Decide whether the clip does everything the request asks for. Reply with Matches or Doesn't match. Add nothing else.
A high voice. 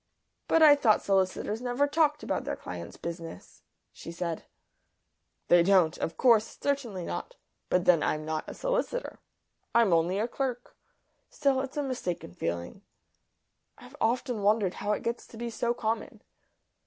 Matches